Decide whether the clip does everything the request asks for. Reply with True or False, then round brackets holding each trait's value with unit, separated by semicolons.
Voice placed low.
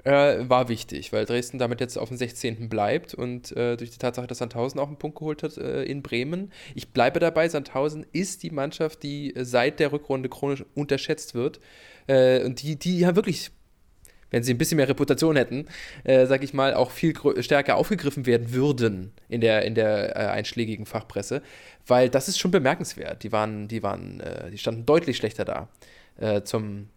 True (130 Hz)